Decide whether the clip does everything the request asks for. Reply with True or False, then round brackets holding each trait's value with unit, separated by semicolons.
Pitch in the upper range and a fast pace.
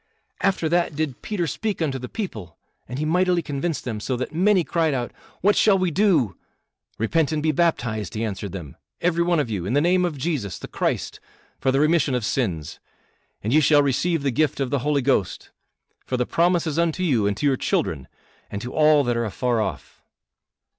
False (145 Hz; 210 wpm)